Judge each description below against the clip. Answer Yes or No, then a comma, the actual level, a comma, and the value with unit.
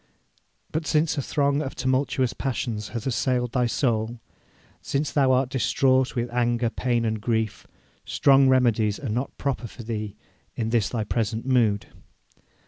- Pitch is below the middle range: Yes, low, 125 Hz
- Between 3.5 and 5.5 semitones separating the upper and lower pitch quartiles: No, average, 2.8 semitones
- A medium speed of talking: Yes, average, 150 wpm